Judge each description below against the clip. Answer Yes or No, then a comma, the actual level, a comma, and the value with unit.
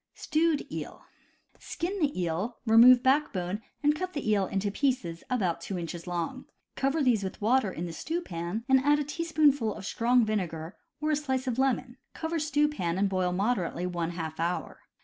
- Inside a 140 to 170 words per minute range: No, average, 190 wpm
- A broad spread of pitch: Yes, wide, 8.0 semitones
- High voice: Yes, high, 230 Hz